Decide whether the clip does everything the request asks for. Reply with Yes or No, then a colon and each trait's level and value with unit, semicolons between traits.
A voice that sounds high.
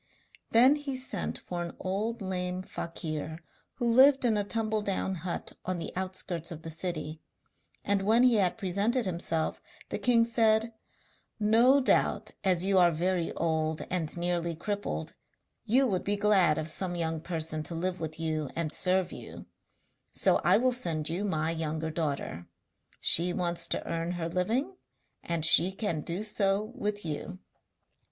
No: medium, 180 Hz